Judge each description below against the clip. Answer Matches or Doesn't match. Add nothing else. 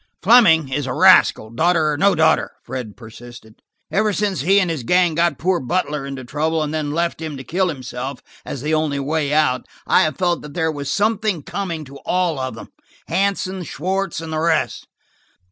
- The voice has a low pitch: Doesn't match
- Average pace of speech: Matches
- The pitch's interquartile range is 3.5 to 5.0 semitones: Matches